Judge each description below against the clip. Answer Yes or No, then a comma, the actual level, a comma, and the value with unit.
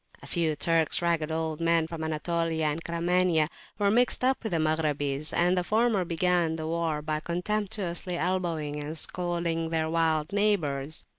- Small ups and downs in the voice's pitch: Yes, narrow, 2.2 semitones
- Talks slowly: No, average, 160 wpm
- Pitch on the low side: No, medium, 165 Hz